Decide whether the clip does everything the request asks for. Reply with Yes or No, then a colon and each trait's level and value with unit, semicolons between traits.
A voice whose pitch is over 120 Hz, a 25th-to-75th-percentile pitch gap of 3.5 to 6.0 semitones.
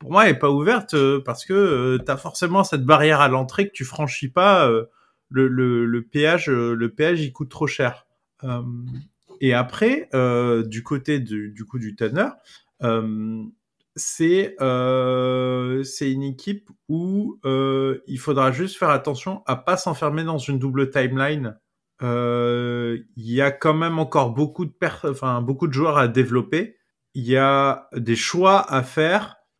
Yes: low, 135 Hz; average, 4.1 semitones